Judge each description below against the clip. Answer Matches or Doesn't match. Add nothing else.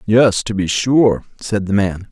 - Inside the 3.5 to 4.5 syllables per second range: Matches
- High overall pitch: Doesn't match